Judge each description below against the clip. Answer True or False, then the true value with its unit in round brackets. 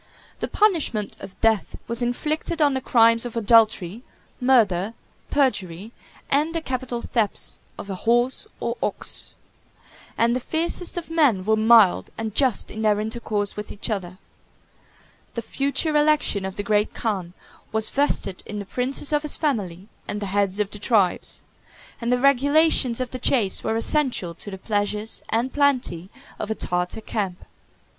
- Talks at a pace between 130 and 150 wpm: False (160 wpm)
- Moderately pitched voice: False (225 Hz)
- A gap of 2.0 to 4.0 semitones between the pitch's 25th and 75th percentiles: False (4.5 semitones)